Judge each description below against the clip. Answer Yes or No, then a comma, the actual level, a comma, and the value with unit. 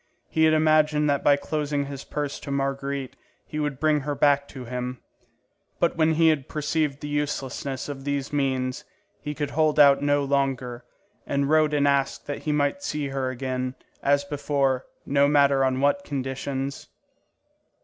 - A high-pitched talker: No, medium, 140 Hz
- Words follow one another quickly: No, average, 170 wpm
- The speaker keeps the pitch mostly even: Yes, narrow, 1.6 semitones